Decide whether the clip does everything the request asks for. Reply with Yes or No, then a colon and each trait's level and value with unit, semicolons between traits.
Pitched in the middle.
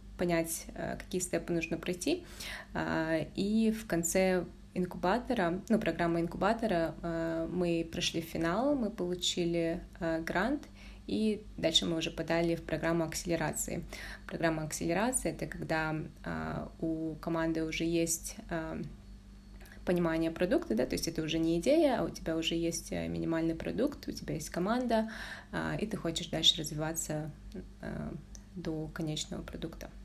Yes: medium, 165 Hz